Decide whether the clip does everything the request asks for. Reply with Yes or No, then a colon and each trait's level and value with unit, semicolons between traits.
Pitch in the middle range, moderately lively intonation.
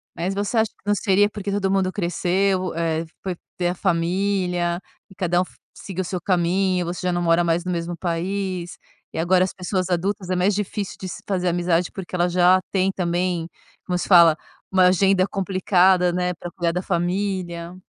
No: medium, 180 Hz; narrow, 1.7 semitones